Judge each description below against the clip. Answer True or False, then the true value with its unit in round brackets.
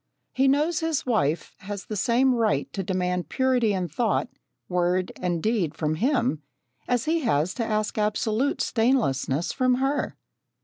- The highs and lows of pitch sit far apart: True (6.2 semitones)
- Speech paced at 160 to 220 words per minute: False (150 wpm)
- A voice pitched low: False (220 Hz)